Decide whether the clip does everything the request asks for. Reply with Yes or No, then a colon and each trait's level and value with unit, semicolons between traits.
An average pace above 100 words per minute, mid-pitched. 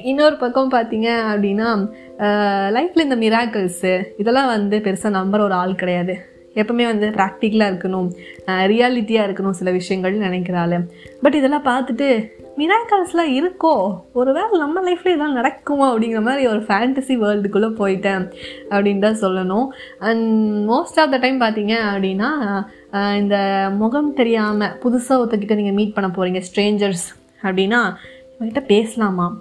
No: fast, 130 wpm; high, 215 Hz